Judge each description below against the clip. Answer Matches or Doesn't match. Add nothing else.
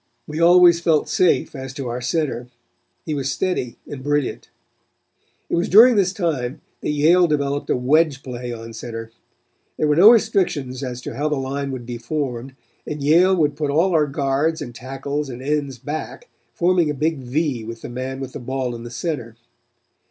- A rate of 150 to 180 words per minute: Doesn't match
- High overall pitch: Doesn't match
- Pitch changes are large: Doesn't match